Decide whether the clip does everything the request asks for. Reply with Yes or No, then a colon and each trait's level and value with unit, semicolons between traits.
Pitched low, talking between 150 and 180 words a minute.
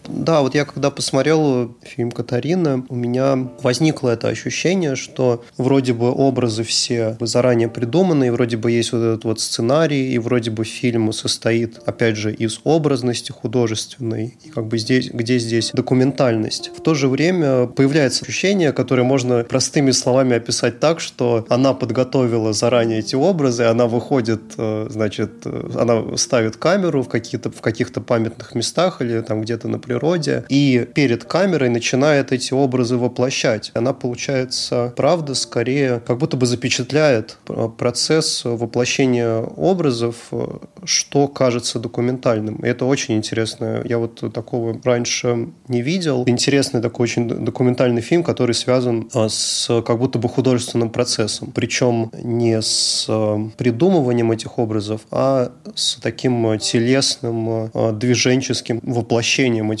No: low, 125 Hz; average, 135 wpm